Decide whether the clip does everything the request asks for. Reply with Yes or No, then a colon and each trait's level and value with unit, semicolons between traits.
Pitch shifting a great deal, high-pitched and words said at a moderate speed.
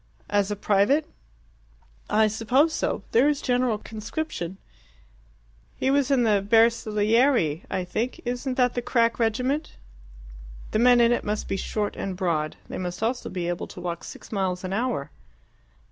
No: average, 4.3 semitones; high, 220 Hz; average, 160 wpm